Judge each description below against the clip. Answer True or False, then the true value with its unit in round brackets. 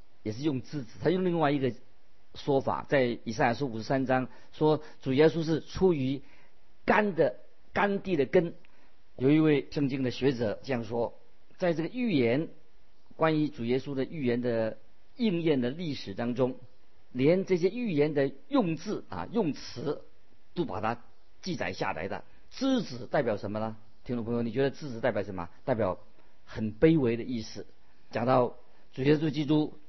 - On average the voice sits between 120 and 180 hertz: True (135 Hz)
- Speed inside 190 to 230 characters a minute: False (245 characters per minute)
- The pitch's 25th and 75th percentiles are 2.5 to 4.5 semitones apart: False (4.9 semitones)